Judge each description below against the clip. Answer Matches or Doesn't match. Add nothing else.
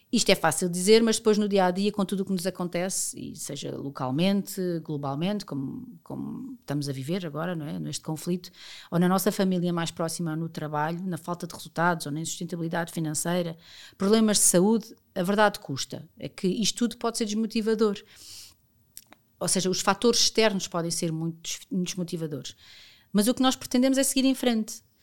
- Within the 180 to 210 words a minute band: Matches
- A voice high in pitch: Doesn't match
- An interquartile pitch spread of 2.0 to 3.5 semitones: Doesn't match